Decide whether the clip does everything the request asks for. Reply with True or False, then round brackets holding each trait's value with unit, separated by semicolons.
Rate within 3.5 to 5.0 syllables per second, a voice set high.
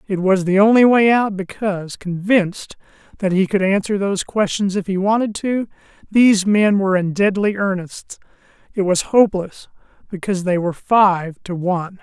False (5.2 syllables/s; 195 Hz)